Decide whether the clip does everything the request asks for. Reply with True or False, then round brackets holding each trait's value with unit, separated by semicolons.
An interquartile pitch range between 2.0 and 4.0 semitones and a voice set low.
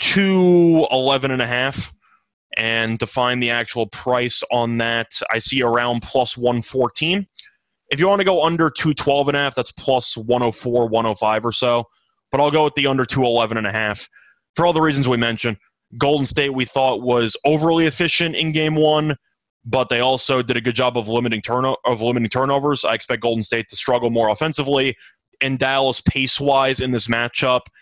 True (3.2 semitones; 125 Hz)